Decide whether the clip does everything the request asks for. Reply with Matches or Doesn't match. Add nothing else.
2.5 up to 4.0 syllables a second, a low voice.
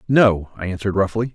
Doesn't match